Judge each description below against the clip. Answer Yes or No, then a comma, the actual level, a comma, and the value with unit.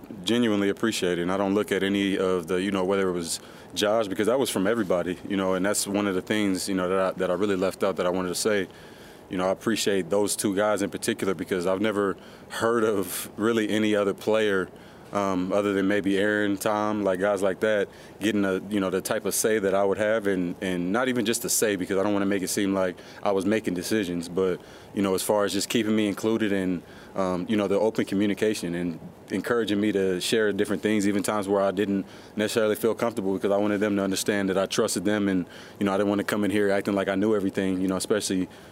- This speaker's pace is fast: Yes, fast, 255 wpm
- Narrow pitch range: Yes, narrow, 1.8 semitones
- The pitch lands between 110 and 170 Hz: No, low, 100 Hz